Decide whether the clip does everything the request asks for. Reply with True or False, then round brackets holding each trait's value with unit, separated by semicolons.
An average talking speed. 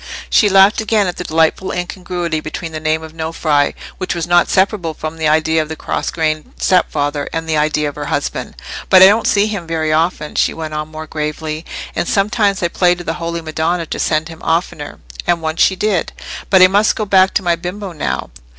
False (210 wpm)